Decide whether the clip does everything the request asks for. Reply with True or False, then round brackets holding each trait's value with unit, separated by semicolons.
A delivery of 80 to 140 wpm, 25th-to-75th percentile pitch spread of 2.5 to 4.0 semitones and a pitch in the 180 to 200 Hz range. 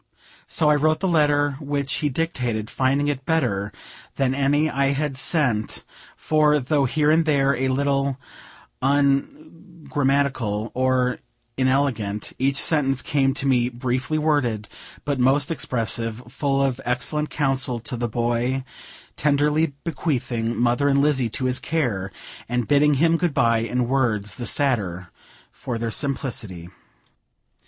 False (135 wpm; 3.2 semitones; 135 Hz)